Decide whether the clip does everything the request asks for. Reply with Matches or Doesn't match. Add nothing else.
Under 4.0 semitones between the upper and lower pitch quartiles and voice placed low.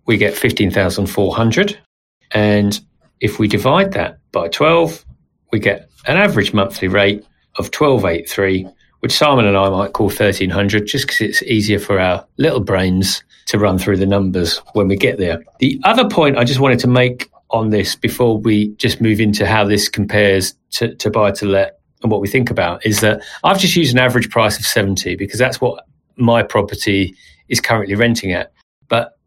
Matches